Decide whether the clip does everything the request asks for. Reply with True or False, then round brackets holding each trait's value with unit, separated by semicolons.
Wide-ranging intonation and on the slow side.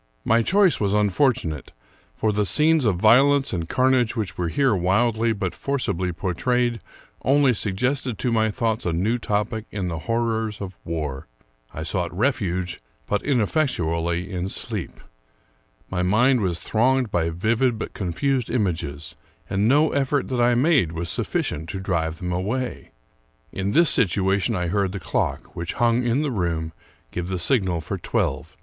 False (5.7 semitones; 160 wpm)